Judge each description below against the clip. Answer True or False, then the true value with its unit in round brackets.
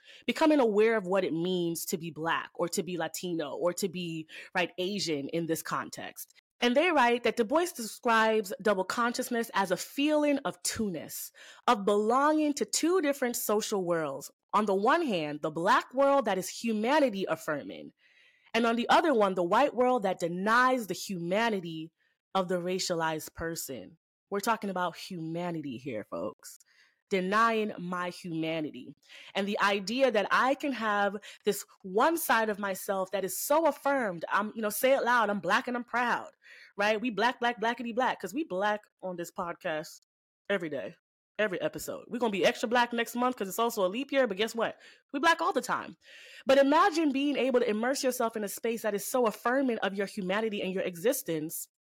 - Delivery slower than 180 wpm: False (190 wpm)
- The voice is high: True (215 Hz)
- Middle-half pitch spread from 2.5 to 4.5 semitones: False (5.2 semitones)